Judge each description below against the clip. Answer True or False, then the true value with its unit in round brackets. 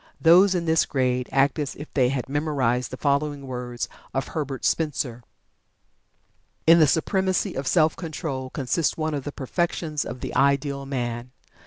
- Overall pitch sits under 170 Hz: True (140 Hz)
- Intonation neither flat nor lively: True (3.4 semitones)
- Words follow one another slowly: False (160 wpm)